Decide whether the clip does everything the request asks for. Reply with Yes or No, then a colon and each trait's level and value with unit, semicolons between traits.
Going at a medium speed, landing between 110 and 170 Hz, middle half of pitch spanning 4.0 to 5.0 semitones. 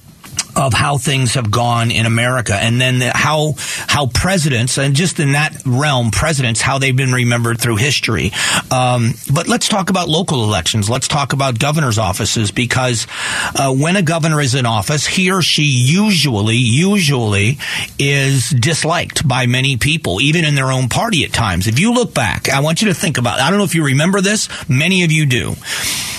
Yes: average, 190 wpm; low, 135 Hz; average, 4.6 semitones